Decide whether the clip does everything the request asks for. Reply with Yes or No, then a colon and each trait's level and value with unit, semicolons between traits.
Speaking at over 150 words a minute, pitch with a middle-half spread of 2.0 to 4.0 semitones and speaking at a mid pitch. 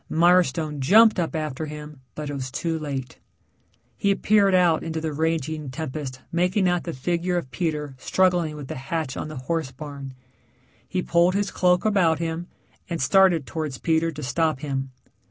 Yes: average, 170 wpm; average, 3.5 semitones; medium, 160 Hz